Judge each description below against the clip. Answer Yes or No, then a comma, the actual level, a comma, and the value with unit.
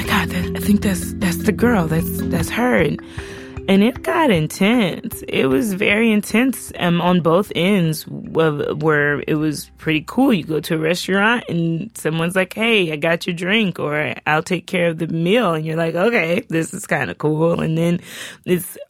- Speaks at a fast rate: No, average, 195 wpm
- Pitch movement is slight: No, average, 4.1 semitones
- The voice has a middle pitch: Yes, medium, 175 Hz